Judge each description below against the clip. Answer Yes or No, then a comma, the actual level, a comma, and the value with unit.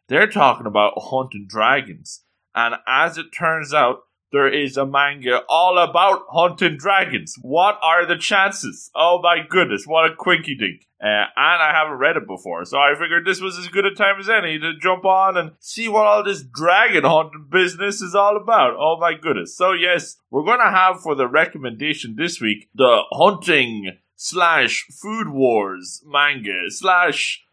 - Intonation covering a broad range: Yes, wide, 6.0 semitones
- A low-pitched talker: No, medium, 165 Hz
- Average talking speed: Yes, average, 180 wpm